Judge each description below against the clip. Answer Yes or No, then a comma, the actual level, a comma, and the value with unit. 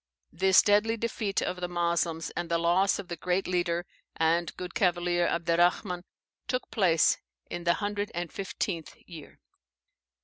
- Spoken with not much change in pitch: Yes, narrow, 2.2 semitones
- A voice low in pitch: No, medium, 175 Hz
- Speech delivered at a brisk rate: No, average, 145 wpm